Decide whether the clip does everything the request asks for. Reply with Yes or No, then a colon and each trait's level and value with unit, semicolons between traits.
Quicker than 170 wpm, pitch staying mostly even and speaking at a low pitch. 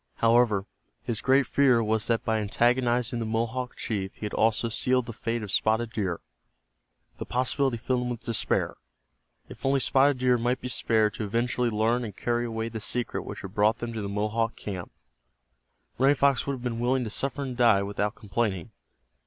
Yes: average, 190 wpm; narrow, 2.3 semitones; low, 115 Hz